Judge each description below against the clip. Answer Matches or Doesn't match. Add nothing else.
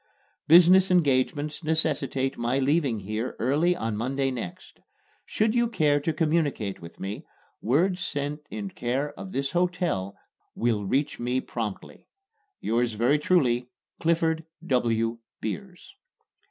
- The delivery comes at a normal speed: Doesn't match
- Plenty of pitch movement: Matches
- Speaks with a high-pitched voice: Doesn't match